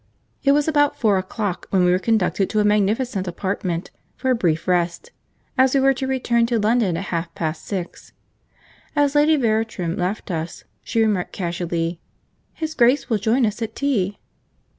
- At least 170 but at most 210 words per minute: Yes, average, 175 wpm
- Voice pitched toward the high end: Yes, high, 210 Hz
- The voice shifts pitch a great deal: Yes, wide, 5.9 semitones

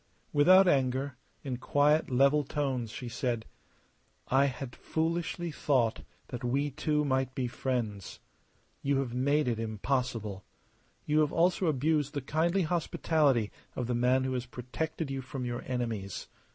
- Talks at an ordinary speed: Yes, average, 145 wpm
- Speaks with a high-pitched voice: No, low, 135 Hz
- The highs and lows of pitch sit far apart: No, average, 3.3 semitones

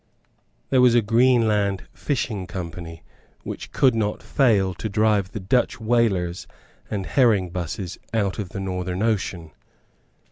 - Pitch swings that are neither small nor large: Yes, average, 3.8 semitones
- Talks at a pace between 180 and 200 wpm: No, slow, 135 wpm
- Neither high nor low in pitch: No, low, 100 Hz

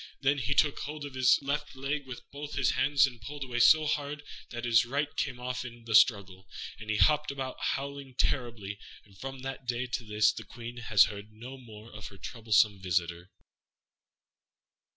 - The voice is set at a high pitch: No, low, 125 Hz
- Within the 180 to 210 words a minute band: Yes, average, 190 wpm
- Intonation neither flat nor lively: Yes, average, 4.3 semitones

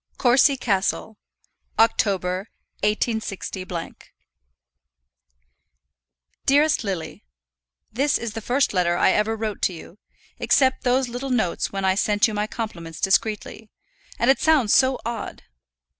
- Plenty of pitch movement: No, average, 4.2 semitones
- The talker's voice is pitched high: Yes, high, 220 Hz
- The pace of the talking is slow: Yes, slow, 120 wpm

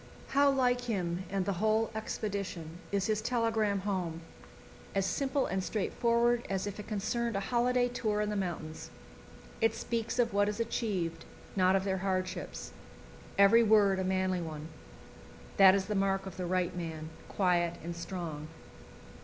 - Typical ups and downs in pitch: Yes, average, 3.3 semitones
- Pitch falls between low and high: No, high, 195 Hz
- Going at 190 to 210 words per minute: No, average, 160 wpm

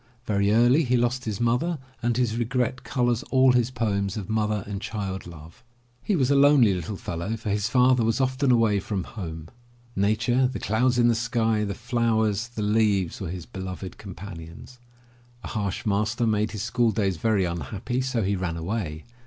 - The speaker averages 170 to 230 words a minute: Yes, average, 185 wpm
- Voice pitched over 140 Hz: No, low, 110 Hz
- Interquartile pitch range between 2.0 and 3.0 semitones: No, average, 3.7 semitones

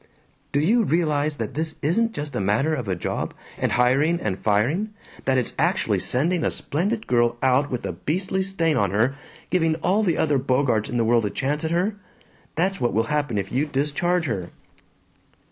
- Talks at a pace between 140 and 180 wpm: No, average, 195 wpm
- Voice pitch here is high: No, medium, 145 Hz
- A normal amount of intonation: No, wide, 6.1 semitones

